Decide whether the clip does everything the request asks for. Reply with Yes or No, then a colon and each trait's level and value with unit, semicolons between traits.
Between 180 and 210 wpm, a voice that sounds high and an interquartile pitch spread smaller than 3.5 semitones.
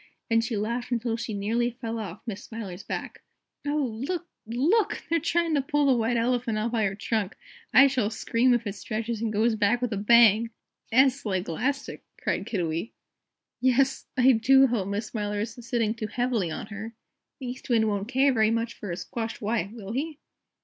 Yes: average, 195 wpm; high, 230 Hz; average, 2.8 semitones